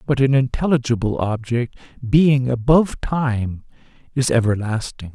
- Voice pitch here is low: Yes, low, 125 Hz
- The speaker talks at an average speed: No, slow, 105 wpm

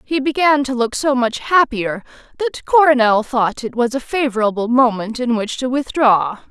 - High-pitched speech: Yes, very high, 250 Hz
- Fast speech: No, average, 175 wpm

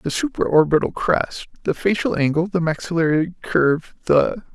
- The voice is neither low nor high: Yes, medium, 165 Hz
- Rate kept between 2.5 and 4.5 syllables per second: No, 4.9 syllables/s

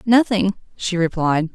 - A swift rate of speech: No, slow, 115 wpm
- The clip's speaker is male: No, female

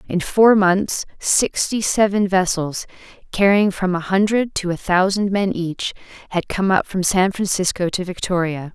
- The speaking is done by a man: No, female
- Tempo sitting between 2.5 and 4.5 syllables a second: Yes, 4.3 syllables/s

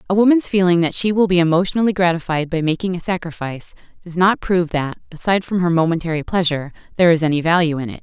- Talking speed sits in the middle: No, fast, 210 wpm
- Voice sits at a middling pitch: Yes, medium, 175 Hz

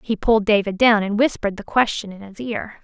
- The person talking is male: No, female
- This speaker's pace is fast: Yes, fast, 235 wpm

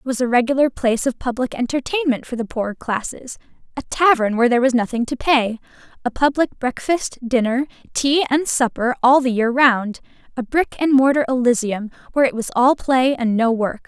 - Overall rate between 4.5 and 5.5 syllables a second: Yes, 5.4 syllables/s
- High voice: Yes, very high, 250 Hz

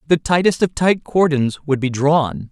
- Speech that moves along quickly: No, average, 190 wpm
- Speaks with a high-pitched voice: No, medium, 150 Hz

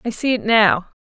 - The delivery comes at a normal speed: No, fast, 230 wpm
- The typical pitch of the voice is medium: No, high, 215 Hz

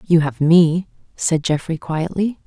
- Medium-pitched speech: Yes, medium, 165 Hz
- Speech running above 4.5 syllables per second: No, 4.0 syllables/s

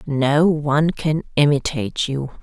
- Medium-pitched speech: Yes, medium, 145 Hz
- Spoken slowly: Yes, slow, 125 wpm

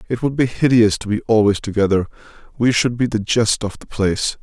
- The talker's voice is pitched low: Yes, low, 110 Hz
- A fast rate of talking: Yes, fast, 215 wpm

